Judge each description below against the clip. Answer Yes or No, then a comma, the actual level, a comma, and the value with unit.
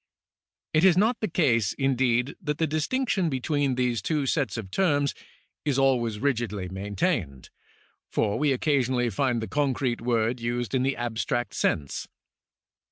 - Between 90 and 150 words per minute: Yes, average, 145 wpm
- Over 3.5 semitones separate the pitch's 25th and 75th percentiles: Yes, average, 4.1 semitones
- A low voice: Yes, low, 130 Hz